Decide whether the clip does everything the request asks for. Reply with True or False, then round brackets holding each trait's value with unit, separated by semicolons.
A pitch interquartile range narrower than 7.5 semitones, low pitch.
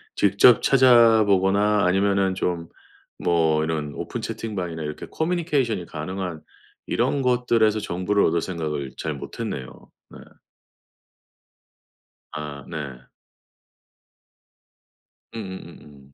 True (5.5 semitones; 95 Hz)